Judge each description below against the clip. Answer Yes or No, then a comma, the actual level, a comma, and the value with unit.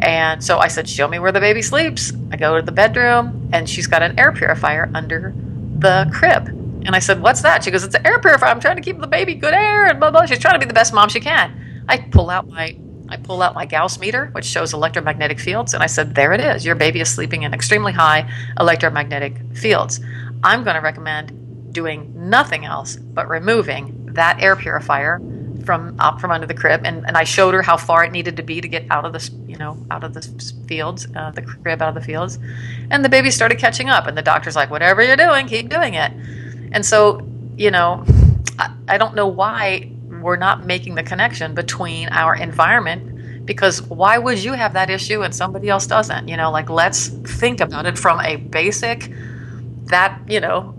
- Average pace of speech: No, fast, 220 wpm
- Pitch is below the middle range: No, medium, 150 Hz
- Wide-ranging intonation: Yes, wide, 5.8 semitones